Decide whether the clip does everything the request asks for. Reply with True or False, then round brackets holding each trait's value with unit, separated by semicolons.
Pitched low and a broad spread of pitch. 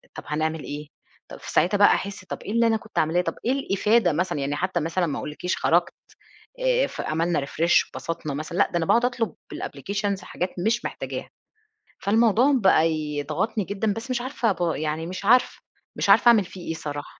False (185 Hz; 5.8 semitones)